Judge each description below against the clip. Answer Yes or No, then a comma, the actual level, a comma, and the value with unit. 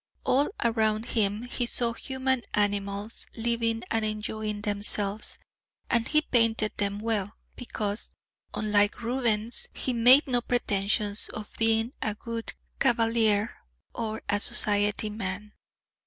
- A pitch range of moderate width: No, narrow, 2.2 semitones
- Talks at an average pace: No, slow, 120 wpm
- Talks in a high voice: Yes, high, 220 Hz